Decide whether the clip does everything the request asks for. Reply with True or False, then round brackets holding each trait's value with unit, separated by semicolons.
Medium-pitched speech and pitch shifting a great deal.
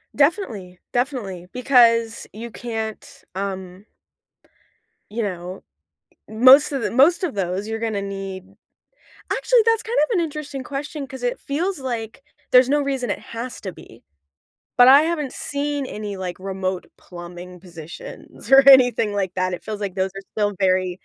False (225 Hz; 6.3 semitones)